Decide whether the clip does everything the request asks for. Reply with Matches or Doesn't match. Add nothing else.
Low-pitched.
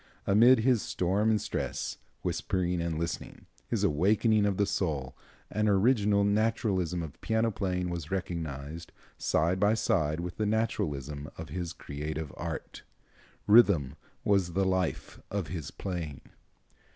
Matches